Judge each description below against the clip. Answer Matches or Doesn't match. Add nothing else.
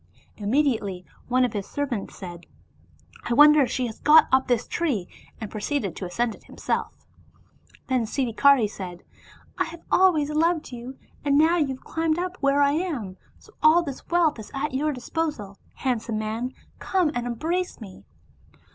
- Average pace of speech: Matches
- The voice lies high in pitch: Matches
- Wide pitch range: Matches